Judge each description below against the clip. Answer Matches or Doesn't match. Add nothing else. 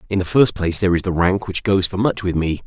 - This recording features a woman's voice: Doesn't match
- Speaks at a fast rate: Matches